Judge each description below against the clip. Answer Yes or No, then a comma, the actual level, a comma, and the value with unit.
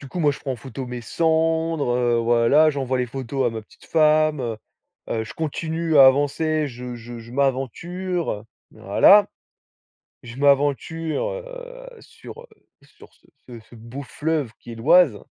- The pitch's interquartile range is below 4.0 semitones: No, average, 5.0 semitones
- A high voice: No, medium, 140 Hz